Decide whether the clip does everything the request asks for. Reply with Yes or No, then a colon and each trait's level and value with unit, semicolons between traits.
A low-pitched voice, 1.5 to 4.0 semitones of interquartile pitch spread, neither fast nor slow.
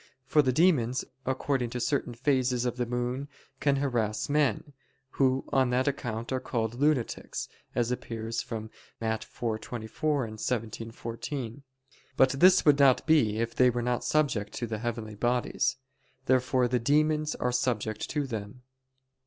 Yes: low, 125 Hz; average, 3.1 semitones; average, 150 wpm